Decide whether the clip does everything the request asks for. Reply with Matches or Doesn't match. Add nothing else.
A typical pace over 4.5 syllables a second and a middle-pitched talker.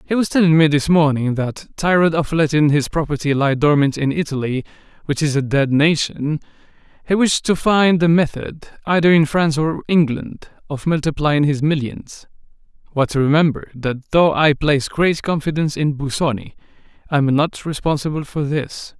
Matches